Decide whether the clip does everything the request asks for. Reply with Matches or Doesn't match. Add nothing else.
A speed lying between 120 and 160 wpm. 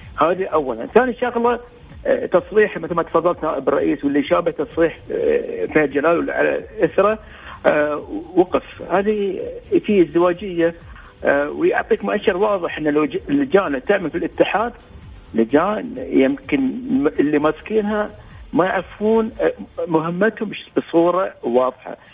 Doesn't match